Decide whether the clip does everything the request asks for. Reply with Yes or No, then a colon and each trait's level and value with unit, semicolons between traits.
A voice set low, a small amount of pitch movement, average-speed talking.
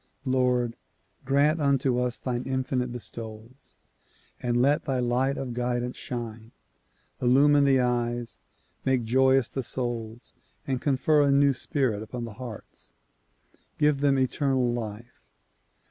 No: low, 125 Hz; narrow, 2.1 semitones; slow, 125 wpm